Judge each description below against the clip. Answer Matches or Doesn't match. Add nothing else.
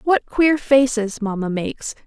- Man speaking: Doesn't match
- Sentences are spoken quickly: Doesn't match